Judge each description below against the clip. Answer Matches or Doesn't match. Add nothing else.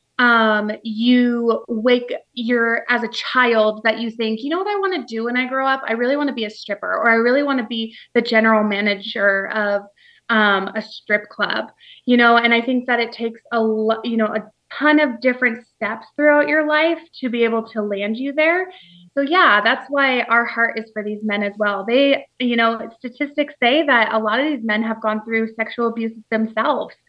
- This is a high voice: Matches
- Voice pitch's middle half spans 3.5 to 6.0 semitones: Doesn't match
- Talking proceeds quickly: Matches